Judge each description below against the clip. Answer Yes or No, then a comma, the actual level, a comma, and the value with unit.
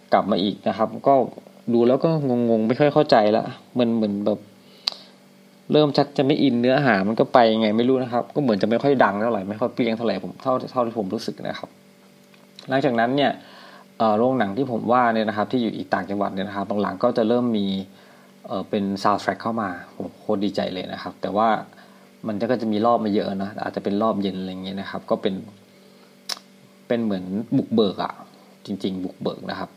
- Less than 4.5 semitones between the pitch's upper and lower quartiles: Yes, average, 3.5 semitones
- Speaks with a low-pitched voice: Yes, low, 110 Hz